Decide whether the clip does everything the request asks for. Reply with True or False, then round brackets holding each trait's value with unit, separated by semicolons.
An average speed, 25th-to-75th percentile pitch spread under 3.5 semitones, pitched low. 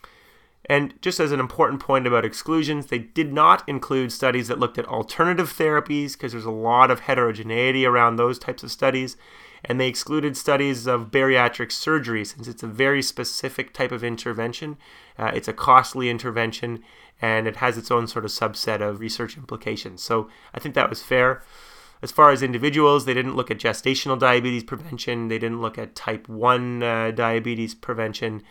True (180 wpm; 2.8 semitones; 125 Hz)